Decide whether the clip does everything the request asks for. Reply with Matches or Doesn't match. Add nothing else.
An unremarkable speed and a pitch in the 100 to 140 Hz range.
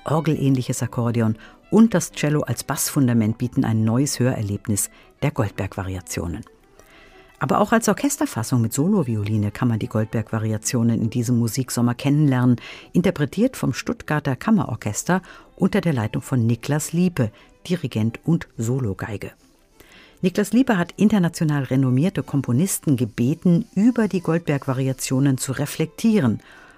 Doesn't match